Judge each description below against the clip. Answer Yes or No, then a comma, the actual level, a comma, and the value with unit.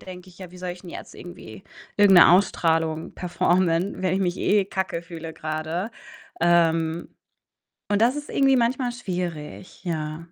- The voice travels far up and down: No, average, 2.8 semitones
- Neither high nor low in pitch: Yes, medium, 175 Hz